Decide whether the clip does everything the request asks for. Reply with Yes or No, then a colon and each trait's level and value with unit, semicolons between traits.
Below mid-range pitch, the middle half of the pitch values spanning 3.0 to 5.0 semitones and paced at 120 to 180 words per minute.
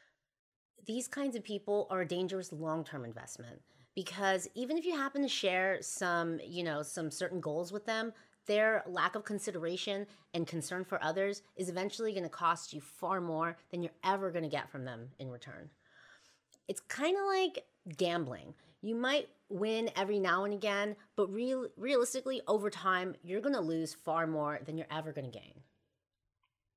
No: high, 190 Hz; average, 4.6 semitones; average, 175 wpm